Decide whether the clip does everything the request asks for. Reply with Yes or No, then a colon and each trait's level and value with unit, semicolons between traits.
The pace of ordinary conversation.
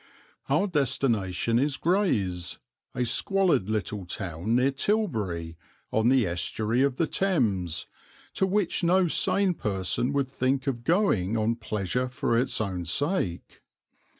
No: slow, 130 wpm